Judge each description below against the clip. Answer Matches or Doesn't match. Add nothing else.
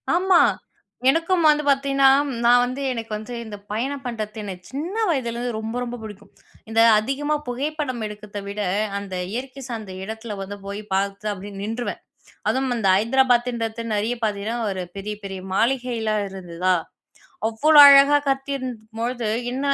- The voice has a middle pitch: Doesn't match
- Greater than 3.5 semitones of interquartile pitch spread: Matches